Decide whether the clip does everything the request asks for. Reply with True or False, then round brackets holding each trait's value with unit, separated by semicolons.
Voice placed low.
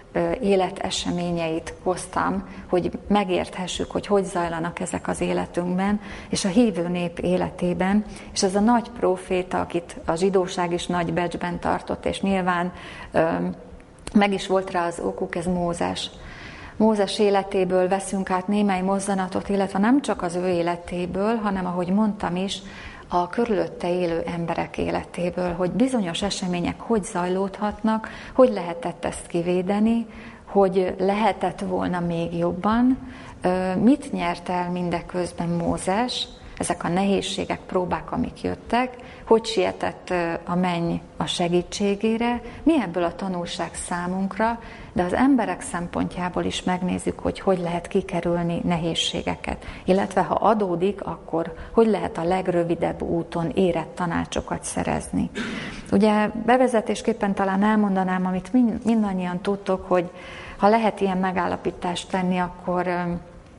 False (185 Hz)